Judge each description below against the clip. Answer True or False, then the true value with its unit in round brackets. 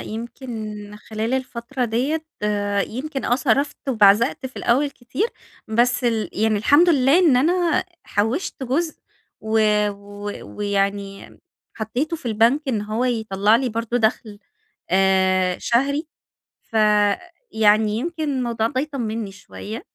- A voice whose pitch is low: False (235 Hz)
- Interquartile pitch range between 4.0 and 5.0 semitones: True (4.3 semitones)